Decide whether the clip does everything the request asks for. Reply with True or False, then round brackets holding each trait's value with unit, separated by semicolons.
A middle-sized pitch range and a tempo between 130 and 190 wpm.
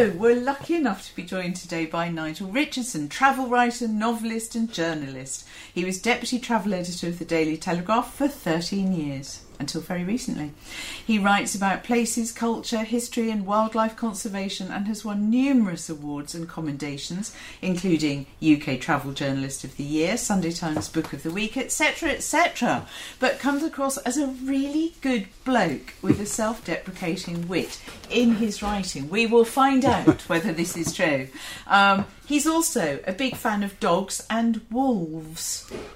False (6.5 semitones; 160 wpm)